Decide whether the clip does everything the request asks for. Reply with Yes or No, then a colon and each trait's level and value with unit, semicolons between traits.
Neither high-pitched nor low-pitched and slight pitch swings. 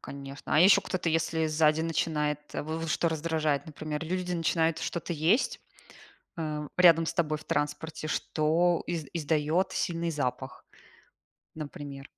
Yes: medium, 160 Hz; narrow, 1.9 semitones